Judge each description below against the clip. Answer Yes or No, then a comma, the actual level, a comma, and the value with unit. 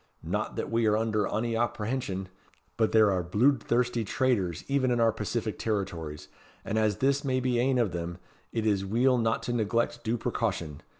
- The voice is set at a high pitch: No, low, 115 Hz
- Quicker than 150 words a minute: Yes, average, 180 wpm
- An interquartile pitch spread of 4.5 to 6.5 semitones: No, average, 3.2 semitones